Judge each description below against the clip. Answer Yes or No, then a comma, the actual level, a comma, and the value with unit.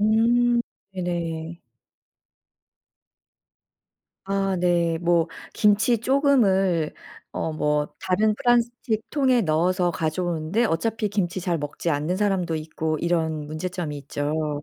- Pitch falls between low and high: Yes, medium, 180 Hz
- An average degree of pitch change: Yes, average, 4.8 semitones